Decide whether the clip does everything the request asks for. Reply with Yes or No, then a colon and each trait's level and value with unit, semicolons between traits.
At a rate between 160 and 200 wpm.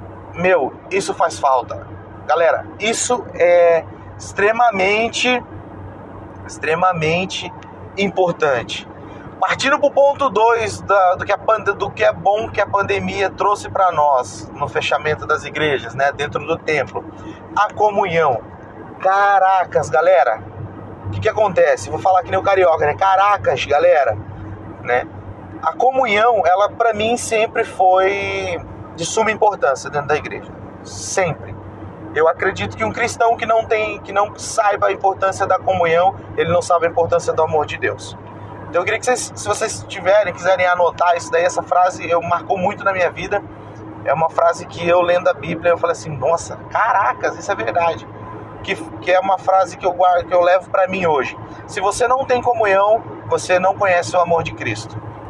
Yes: average, 165 wpm